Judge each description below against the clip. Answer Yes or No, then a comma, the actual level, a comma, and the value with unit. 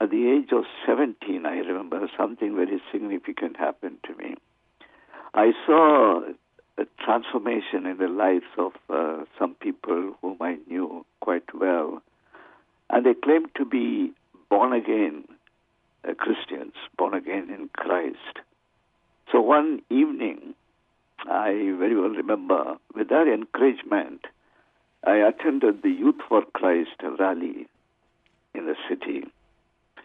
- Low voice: No, very high, 305 Hz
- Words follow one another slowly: Yes, slow, 125 wpm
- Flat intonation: Yes, narrow, 1.6 semitones